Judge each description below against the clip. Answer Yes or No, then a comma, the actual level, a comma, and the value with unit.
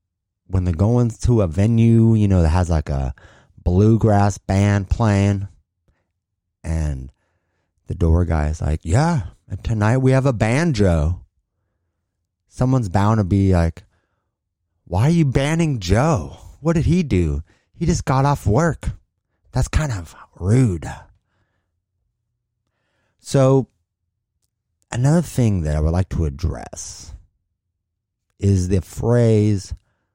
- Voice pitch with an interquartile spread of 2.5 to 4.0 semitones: No, average, 4.4 semitones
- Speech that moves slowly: Yes, slow, 125 wpm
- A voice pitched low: Yes, low, 100 Hz